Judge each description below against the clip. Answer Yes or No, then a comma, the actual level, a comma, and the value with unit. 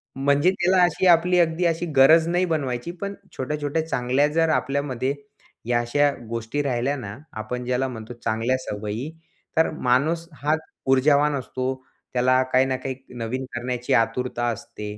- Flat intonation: No, average, 4.3 semitones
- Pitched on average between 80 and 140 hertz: Yes, low, 135 Hz